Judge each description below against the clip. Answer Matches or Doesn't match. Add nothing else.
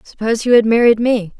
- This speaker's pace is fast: Matches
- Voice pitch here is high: Matches